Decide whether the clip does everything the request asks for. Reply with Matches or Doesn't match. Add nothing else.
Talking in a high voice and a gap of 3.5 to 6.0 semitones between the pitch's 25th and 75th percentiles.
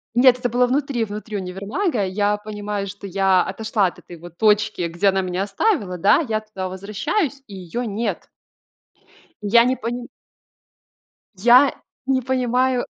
Matches